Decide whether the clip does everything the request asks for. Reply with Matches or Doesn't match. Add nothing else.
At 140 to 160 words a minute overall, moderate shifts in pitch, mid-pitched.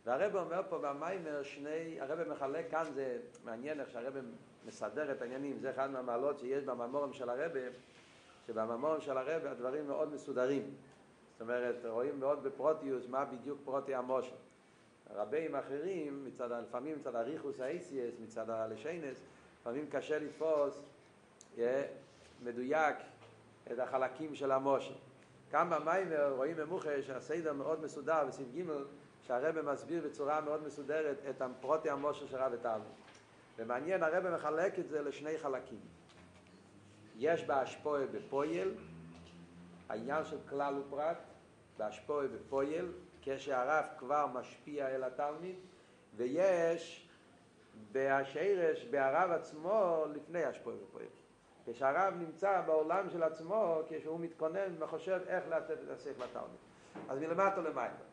Doesn't match